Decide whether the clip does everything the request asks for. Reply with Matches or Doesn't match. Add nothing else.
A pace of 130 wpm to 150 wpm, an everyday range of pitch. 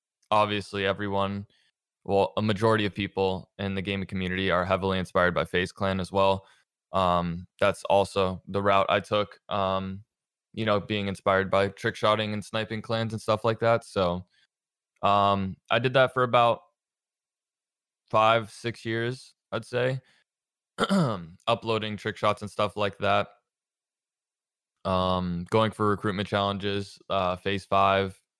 Doesn't match